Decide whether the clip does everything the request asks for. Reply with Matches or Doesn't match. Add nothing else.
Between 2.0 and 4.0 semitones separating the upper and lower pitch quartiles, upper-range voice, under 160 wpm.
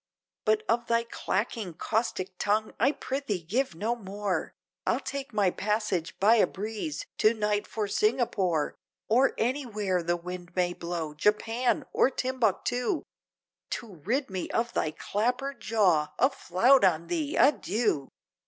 Doesn't match